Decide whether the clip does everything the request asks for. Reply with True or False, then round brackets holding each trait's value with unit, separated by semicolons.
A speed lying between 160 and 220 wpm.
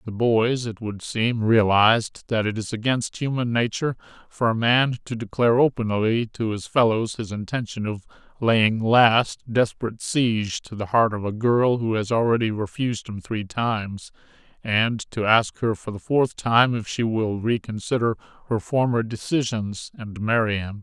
True (170 wpm)